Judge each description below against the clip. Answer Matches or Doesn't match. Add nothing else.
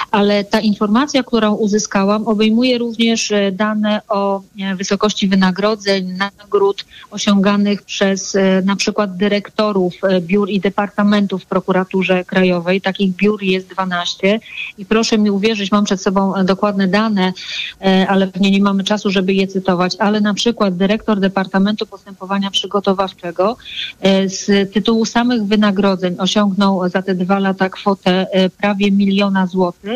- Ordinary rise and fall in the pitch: Doesn't match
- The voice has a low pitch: Doesn't match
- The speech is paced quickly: Doesn't match